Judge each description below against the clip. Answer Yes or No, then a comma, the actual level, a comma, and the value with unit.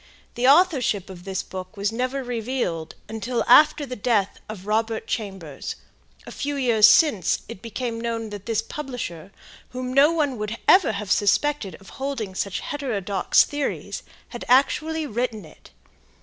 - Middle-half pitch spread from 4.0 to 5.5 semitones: Yes, average, 5.0 semitones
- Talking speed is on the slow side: No, average, 150 wpm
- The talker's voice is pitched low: No, high, 230 Hz